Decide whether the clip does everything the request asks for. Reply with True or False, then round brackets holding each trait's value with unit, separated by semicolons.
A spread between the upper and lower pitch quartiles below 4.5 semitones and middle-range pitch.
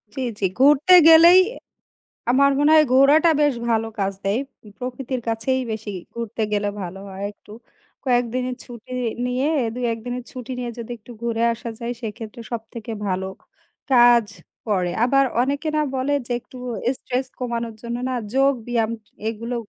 False (2.7 semitones; 245 Hz)